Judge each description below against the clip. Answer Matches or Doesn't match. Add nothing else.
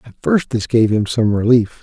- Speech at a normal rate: Doesn't match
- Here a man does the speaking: Matches